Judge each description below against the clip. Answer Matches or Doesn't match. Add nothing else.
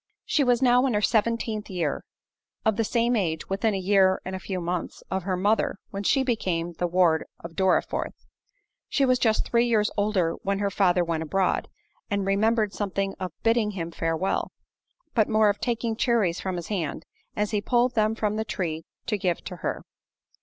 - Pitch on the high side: Matches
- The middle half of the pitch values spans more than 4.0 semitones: Doesn't match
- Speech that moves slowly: Doesn't match